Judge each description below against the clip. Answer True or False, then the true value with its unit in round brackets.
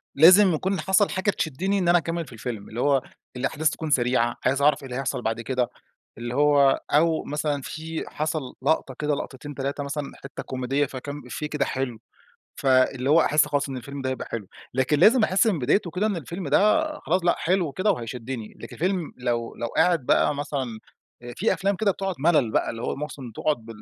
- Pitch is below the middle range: False (145 Hz)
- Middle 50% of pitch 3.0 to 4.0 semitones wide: False (4.6 semitones)